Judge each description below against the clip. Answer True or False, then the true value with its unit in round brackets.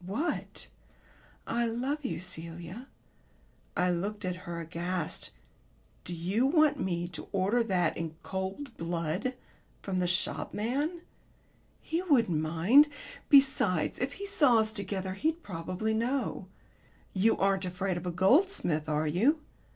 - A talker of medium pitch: False (195 Hz)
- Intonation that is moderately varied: False (6.6 semitones)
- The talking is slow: True (130 wpm)